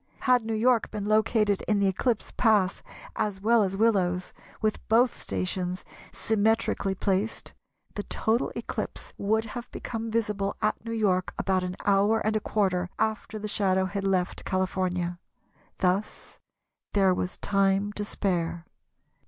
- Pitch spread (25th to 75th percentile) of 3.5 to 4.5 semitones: No, average, 2.7 semitones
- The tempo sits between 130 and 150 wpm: Yes, average, 145 wpm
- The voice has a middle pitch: No, high, 205 Hz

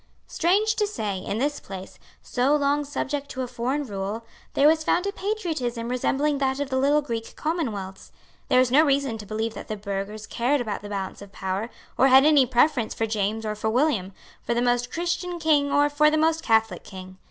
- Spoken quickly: Yes, fast, 210 wpm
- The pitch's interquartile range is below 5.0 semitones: No, wide, 5.4 semitones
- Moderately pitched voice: No, very high, 255 Hz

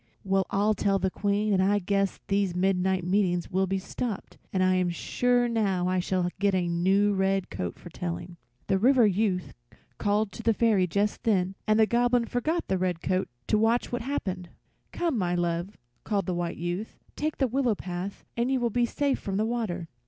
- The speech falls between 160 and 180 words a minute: No, average, 195 wpm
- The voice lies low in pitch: No, high, 195 Hz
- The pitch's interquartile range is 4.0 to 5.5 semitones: No, average, 3.6 semitones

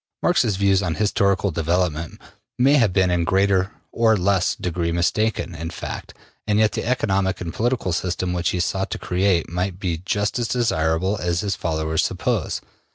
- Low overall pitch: Yes, very low, 95 Hz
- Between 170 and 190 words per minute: Yes, average, 175 wpm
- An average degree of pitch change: Yes, average, 3.0 semitones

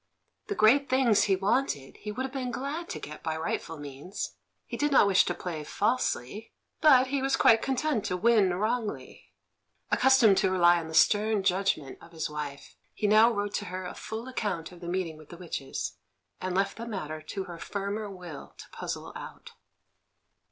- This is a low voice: No, high, 200 Hz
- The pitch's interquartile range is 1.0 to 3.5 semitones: No, wide, 5.4 semitones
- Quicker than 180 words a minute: Yes, average, 190 wpm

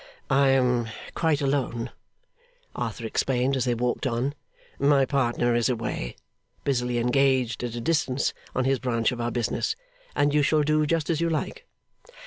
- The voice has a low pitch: Yes, low, 130 Hz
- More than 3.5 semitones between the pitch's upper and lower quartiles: No, average, 3.1 semitones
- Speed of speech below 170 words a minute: Yes, average, 160 wpm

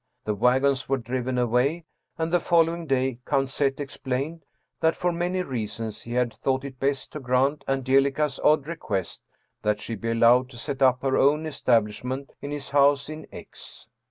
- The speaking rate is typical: Yes, average, 175 wpm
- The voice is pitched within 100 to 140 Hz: Yes, low, 135 Hz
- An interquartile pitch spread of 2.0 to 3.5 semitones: Yes, average, 2.9 semitones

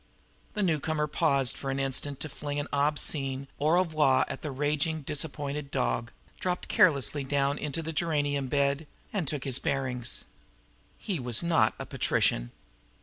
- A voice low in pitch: No, medium, 145 Hz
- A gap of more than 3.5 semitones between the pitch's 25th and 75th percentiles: No, narrow, 2.4 semitones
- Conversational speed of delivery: Yes, average, 145 wpm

